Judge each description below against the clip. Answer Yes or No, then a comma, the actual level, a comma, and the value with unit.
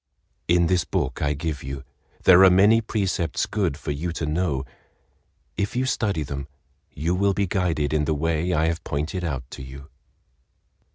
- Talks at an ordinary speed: Yes, average, 170 wpm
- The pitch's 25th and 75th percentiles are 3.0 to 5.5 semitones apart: Yes, average, 4.1 semitones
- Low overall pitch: Yes, very low, 80 Hz